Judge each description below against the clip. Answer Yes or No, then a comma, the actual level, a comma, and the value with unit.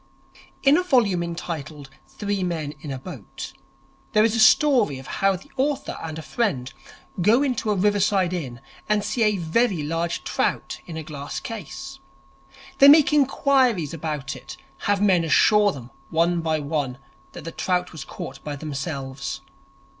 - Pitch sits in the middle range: Yes, medium, 175 Hz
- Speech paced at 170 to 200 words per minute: No, average, 160 wpm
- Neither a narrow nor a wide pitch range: No, wide, 6.3 semitones